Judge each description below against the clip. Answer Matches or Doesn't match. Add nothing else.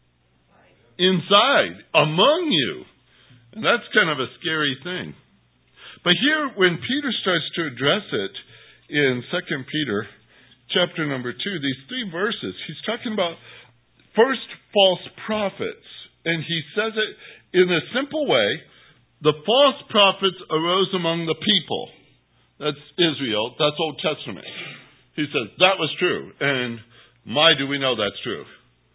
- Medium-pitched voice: Matches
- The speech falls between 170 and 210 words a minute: Doesn't match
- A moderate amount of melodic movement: Doesn't match